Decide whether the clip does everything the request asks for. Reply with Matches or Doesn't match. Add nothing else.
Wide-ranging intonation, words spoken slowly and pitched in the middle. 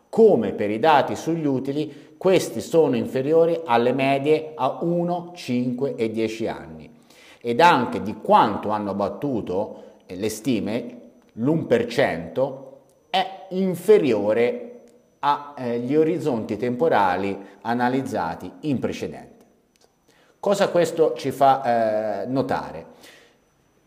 Matches